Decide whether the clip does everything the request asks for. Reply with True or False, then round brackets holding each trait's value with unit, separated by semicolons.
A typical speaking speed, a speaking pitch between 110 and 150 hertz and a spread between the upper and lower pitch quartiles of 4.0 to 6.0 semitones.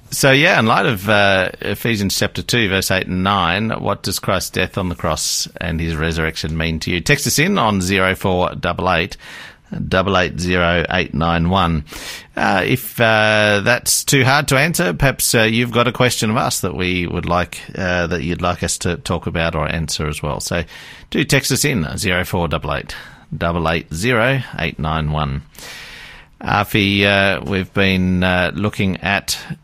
False (185 wpm; 95 Hz; 4.7 semitones)